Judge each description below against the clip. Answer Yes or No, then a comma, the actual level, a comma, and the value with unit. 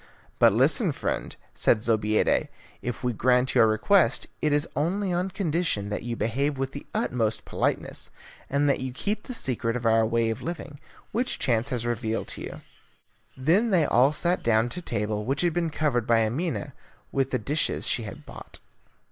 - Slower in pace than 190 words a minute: Yes, average, 180 wpm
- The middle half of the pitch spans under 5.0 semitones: No, wide, 5.6 semitones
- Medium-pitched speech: No, low, 130 Hz